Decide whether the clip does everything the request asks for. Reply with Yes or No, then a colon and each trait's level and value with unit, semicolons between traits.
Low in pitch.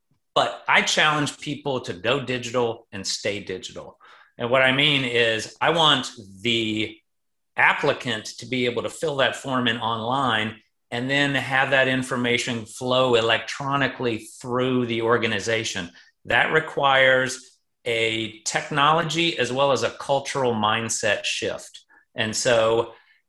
Yes: low, 120 Hz